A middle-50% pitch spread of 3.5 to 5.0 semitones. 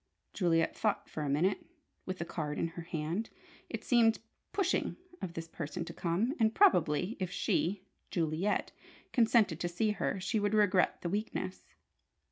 Yes: average, 4.4 semitones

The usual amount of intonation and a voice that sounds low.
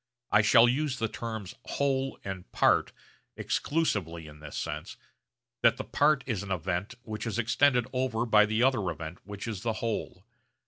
Yes: average, 4.6 semitones; low, 110 Hz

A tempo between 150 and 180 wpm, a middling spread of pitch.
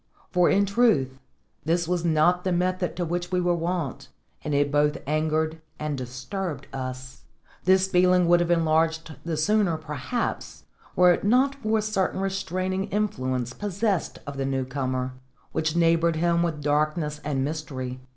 Yes: average, 160 wpm; average, 3.8 semitones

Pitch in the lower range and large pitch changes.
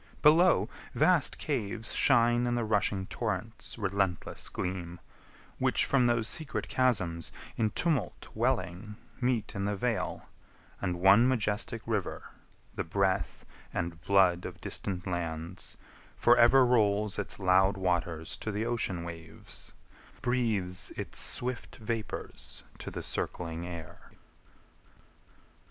No: low, 105 Hz; average, 4.8 semitones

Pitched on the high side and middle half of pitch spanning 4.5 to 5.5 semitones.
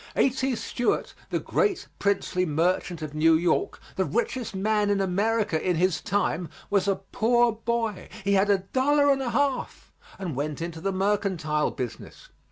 Yes: high, 195 Hz; average, 4.9 semitones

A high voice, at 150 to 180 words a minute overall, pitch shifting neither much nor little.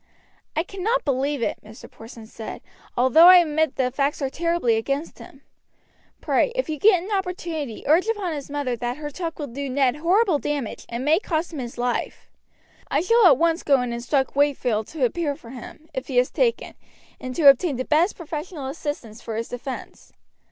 No: very high, 290 Hz; average, 195 wpm; average, 5.0 semitones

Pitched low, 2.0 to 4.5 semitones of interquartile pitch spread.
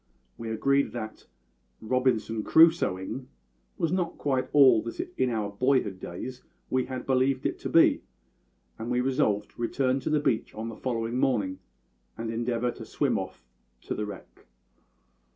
Yes: low, 125 Hz; average, 3.2 semitones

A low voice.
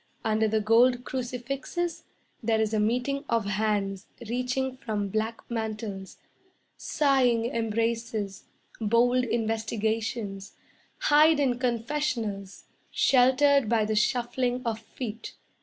No: high, 230 Hz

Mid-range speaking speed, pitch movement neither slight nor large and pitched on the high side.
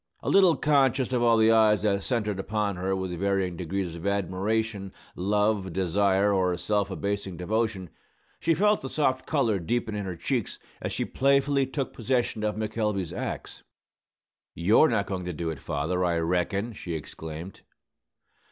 No: average, 160 wpm; average, 3.8 semitones; low, 100 Hz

